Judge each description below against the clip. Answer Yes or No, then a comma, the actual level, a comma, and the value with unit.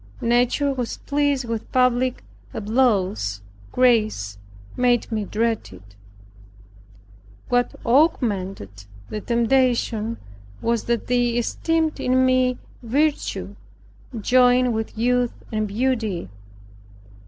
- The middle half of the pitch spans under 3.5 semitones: Yes, average, 2.8 semitones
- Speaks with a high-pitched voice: Yes, high, 240 Hz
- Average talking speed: No, slow, 95 wpm